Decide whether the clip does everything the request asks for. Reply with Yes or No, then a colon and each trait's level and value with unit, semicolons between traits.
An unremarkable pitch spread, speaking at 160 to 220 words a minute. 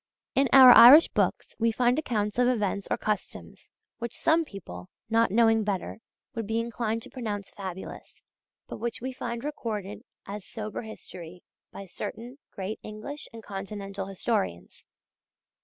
No: average, 3.2 semitones; average, 145 wpm